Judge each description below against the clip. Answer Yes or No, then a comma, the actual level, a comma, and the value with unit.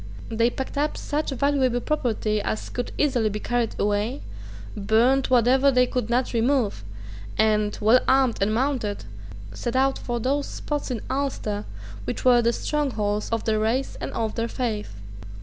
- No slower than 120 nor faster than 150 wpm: No, average, 160 wpm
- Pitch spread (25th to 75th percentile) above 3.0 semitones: Yes, average, 3.6 semitones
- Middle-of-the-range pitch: No, high, 240 Hz